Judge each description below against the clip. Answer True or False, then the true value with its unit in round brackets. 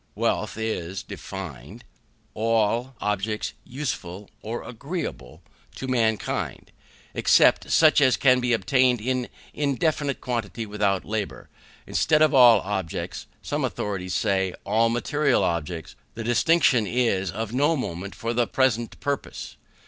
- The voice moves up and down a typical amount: True (4.7 semitones)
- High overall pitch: False (115 Hz)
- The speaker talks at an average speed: False (125 wpm)